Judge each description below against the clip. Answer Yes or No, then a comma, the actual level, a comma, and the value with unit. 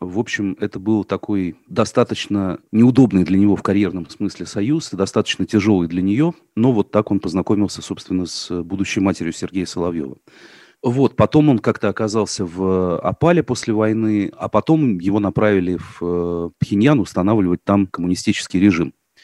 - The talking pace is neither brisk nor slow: Yes, average, 145 wpm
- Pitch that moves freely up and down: No, average, 2.9 semitones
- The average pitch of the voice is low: Yes, low, 100 Hz